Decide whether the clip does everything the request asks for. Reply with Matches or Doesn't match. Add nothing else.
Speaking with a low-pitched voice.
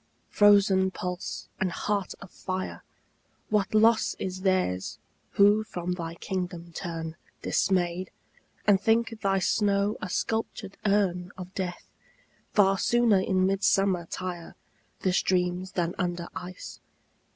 Doesn't match